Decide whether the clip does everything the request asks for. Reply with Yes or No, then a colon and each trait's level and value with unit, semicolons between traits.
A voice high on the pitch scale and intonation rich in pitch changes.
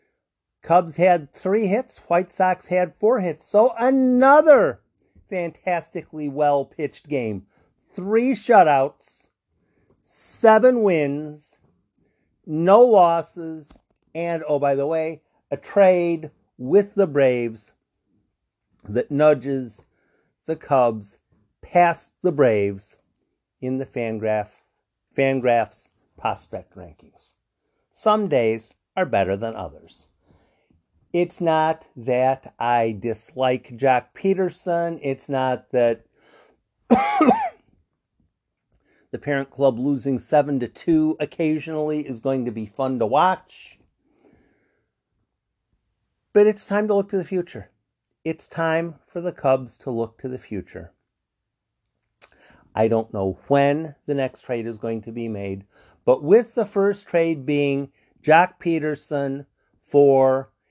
No: medium, 145 Hz; wide, 6.3 semitones